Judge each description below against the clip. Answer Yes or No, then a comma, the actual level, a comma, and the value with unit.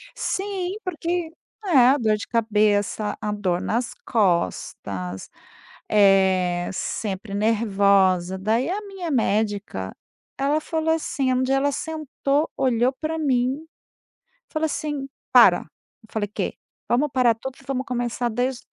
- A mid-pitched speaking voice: No, high, 240 Hz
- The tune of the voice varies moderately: No, wide, 6.2 semitones